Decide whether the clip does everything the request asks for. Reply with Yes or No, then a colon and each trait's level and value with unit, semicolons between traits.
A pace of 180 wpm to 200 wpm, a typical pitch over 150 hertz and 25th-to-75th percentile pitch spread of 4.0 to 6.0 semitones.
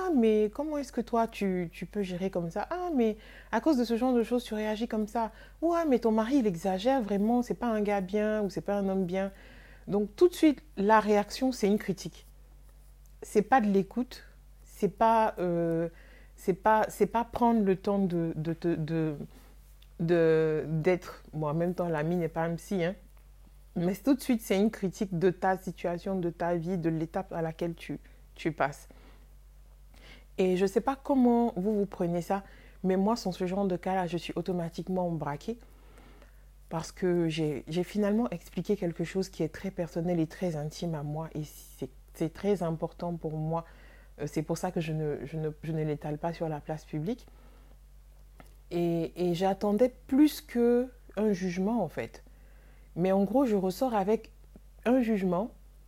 Yes: average, 190 wpm; high, 190 Hz; average, 4.5 semitones